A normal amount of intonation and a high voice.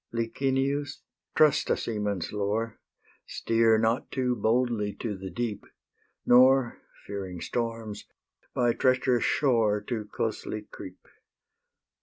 No: average, 3.2 semitones; low, 115 Hz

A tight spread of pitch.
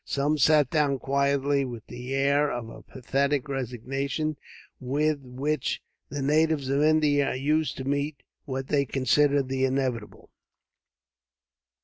Yes: narrow, 1.9 semitones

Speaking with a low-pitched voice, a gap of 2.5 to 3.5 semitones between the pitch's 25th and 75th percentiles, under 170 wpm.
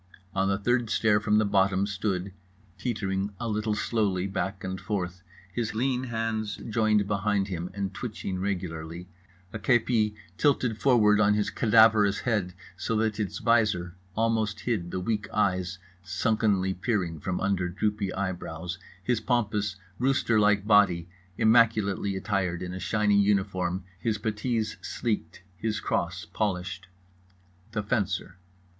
Yes: low, 100 Hz; average, 2.9 semitones; slow, 135 wpm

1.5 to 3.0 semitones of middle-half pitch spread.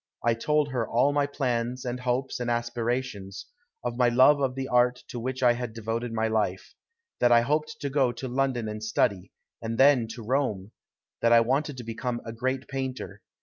Yes: narrow, 2.4 semitones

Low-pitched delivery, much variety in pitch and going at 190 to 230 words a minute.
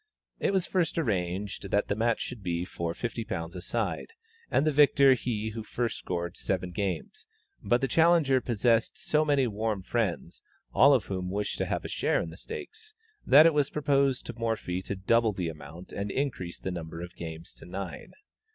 Yes: low, 110 Hz; wide, 6.9 semitones; average, 195 wpm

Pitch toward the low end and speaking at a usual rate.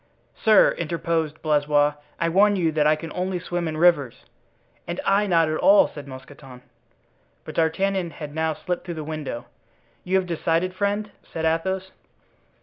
No: medium, 165 Hz; average, 160 wpm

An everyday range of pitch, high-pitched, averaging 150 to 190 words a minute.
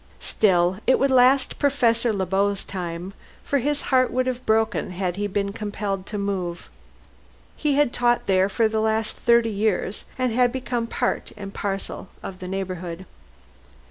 Yes: average, 4.2 semitones; high, 210 Hz; average, 165 wpm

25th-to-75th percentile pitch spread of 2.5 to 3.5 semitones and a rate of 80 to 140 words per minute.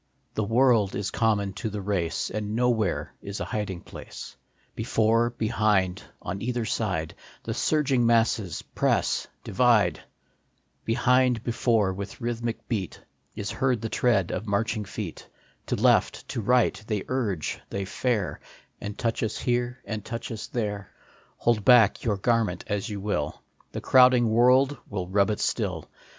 No: average, 3.0 semitones; average, 150 wpm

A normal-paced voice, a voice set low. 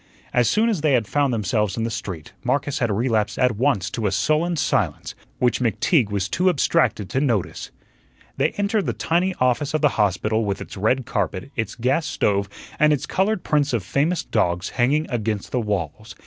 Yes: average, 190 wpm; low, 120 Hz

